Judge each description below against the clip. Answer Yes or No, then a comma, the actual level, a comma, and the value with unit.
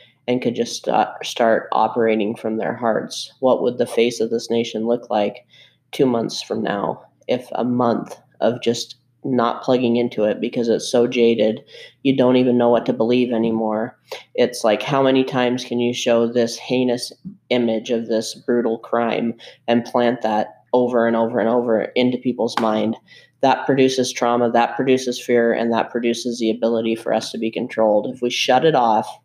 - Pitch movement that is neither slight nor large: No, narrow, 1.6 semitones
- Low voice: Yes, low, 120 Hz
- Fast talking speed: No, average, 185 wpm